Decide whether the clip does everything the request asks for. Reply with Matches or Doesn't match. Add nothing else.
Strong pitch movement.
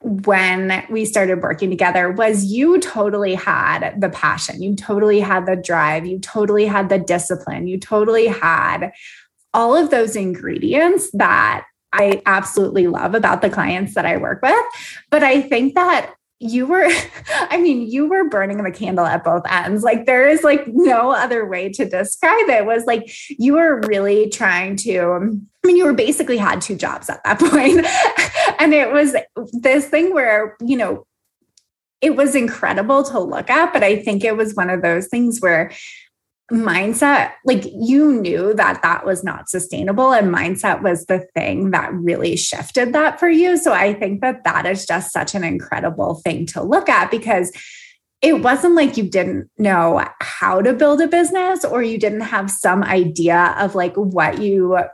Matches